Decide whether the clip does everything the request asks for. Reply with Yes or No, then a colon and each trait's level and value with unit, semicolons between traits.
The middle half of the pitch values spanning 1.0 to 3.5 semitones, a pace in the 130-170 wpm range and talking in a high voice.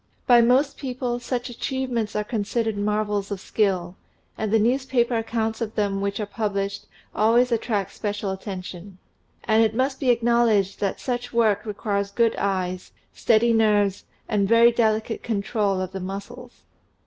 Yes: average, 3.0 semitones; average, 155 wpm; high, 220 Hz